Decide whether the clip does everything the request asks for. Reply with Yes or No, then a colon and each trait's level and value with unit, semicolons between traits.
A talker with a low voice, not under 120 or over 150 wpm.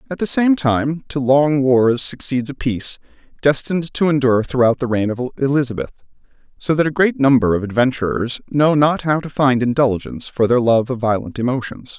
No: low, 130 Hz; average, 185 wpm